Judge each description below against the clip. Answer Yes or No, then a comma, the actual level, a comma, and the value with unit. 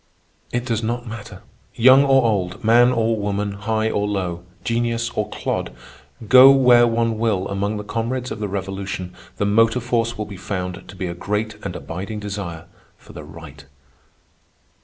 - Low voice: Yes, low, 110 Hz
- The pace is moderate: Yes, average, 170 wpm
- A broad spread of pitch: No, average, 3.0 semitones